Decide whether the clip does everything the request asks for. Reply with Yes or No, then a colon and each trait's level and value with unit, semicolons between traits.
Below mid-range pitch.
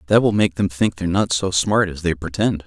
Yes: very low, 90 Hz